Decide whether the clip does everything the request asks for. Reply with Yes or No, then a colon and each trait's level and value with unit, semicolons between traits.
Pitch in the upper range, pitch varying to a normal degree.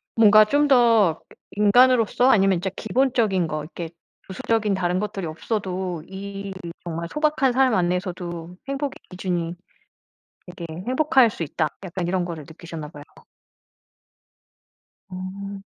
Yes: high, 195 Hz; average, 4.7 semitones